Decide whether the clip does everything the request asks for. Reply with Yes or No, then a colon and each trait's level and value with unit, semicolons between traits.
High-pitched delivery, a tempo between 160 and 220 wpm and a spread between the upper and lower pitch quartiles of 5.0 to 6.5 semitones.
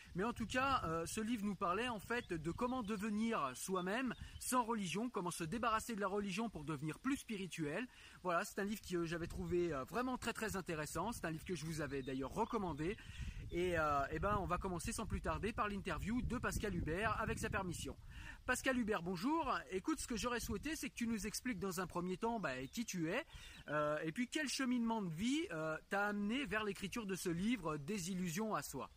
Yes: high, 200 Hz; average, 205 wpm; wide, 5.4 semitones